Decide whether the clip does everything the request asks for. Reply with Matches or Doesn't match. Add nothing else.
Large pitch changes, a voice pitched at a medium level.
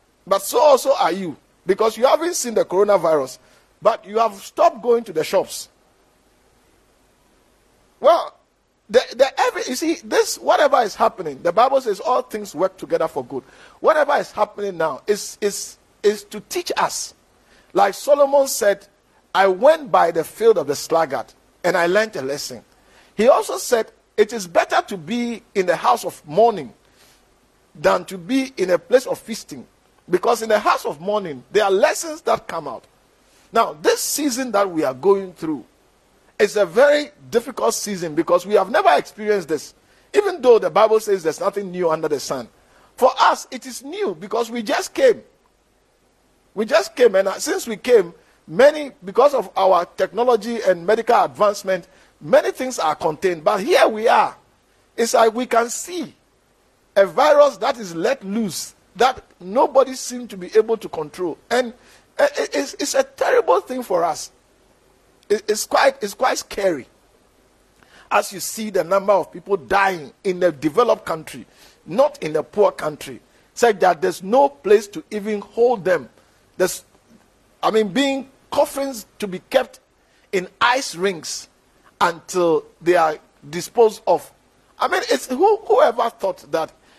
Doesn't match